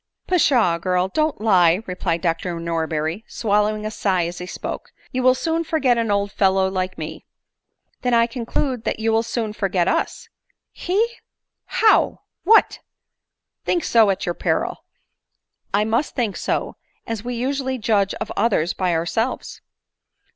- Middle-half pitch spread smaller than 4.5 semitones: No, average, 5.3 semitones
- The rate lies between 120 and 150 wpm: No, average, 160 wpm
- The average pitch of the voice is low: No, high, 215 Hz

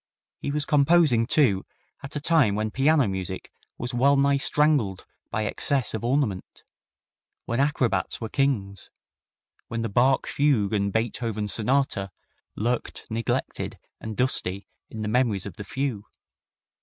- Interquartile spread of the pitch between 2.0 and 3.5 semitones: No, average, 5.0 semitones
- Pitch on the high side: No, low, 120 Hz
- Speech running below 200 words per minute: Yes, average, 140 wpm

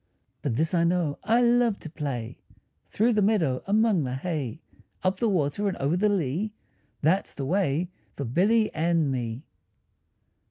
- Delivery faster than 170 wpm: No, average, 160 wpm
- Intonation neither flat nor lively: No, wide, 6.5 semitones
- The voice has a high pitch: No, medium, 170 Hz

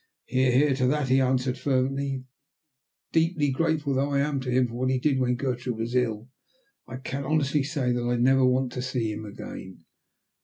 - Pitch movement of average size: No, narrow, 2.0 semitones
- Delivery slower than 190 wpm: No, average, 195 wpm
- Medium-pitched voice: No, low, 130 Hz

